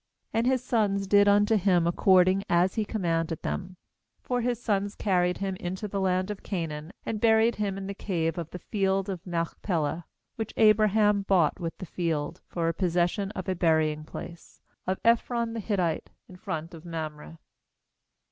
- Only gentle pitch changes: No, average, 3.5 semitones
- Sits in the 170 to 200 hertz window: Yes, high, 190 Hz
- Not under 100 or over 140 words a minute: No, average, 175 wpm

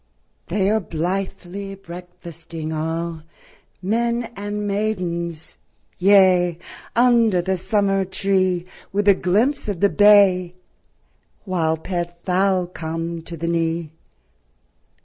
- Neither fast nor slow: No, slow, 100 wpm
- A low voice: No, medium, 185 Hz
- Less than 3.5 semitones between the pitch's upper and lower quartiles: Yes, average, 2.9 semitones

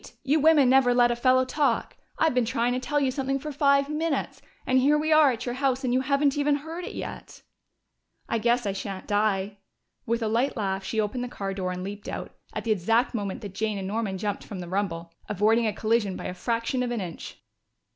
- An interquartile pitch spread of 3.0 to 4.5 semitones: No, average, 4.9 semitones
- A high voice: Yes, high, 235 Hz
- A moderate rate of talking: No, fast, 225 wpm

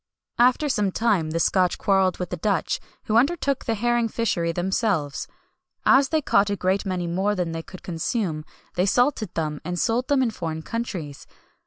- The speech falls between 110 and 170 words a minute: No, average, 180 wpm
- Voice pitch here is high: Yes, high, 195 Hz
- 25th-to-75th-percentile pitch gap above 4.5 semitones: Yes, average, 5.3 semitones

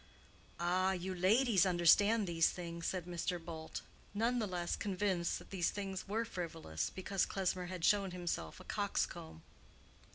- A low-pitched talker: No, medium, 180 Hz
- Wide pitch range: No, narrow, 2.4 semitones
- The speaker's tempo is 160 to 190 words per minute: No, average, 150 wpm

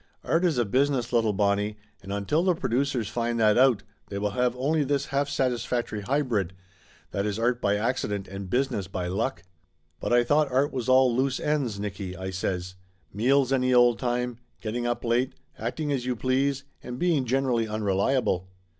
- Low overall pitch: Yes, low, 120 Hz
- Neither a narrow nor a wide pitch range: Yes, average, 4.4 semitones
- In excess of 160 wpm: Yes, average, 180 wpm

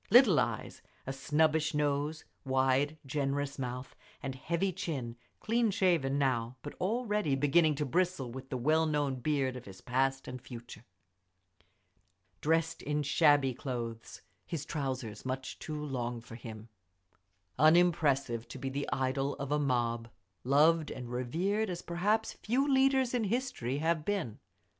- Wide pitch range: No, average, 4.3 semitones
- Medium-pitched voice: Yes, medium, 145 Hz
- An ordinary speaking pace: Yes, average, 145 wpm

